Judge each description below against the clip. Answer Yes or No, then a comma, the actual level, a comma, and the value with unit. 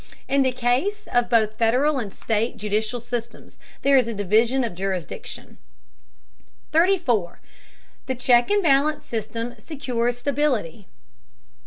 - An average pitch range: Yes, average, 3.7 semitones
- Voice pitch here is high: Yes, high, 240 Hz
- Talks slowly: Yes, slow, 125 wpm